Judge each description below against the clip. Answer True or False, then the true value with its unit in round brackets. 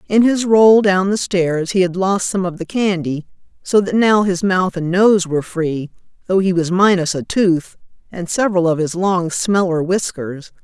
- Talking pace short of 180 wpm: False (200 wpm)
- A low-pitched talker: False (185 Hz)